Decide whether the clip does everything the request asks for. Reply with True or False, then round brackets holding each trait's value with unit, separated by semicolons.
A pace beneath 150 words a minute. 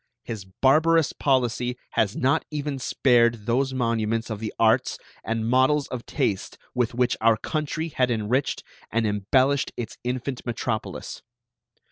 True (135 wpm)